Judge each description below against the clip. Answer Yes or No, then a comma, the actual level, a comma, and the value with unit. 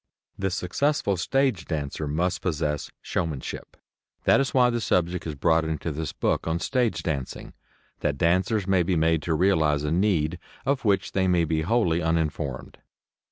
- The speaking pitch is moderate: No, very low, 85 Hz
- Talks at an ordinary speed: Yes, average, 160 wpm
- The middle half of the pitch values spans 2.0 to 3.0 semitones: No, average, 3.7 semitones